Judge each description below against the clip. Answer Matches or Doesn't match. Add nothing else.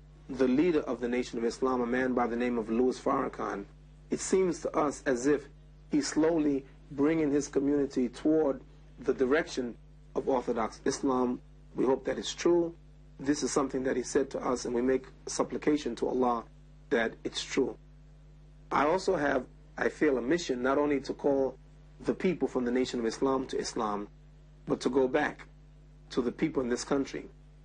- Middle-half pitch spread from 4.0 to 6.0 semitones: Doesn't match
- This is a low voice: Doesn't match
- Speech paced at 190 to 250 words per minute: Doesn't match